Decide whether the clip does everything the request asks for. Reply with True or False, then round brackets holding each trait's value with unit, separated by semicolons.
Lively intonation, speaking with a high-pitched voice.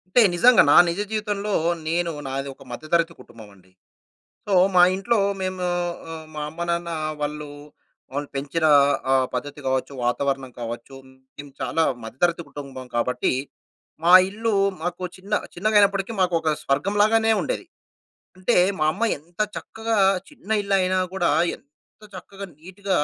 False (5.8 semitones; 170 Hz)